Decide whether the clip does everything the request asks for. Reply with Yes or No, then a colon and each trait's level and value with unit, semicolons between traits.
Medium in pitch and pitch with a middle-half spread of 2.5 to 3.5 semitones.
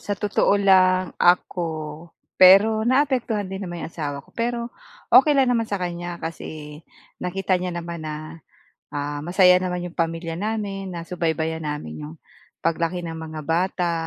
Yes: medium, 175 Hz; average, 3.2 semitones